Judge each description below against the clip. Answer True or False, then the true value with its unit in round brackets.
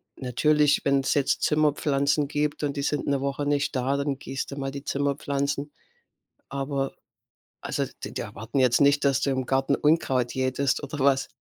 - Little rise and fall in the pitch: True (1.2 semitones)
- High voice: False (140 Hz)